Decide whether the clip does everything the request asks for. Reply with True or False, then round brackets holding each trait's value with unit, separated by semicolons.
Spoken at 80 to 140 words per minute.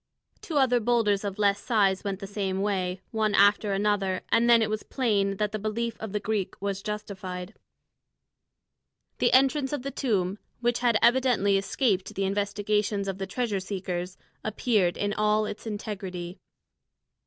False (160 wpm)